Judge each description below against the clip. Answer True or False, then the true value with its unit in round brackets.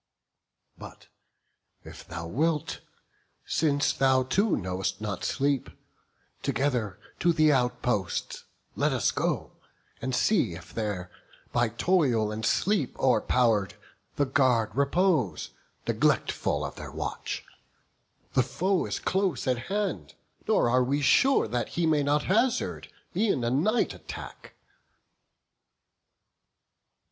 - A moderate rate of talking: False (115 wpm)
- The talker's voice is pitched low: True (130 Hz)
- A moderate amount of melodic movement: False (6.3 semitones)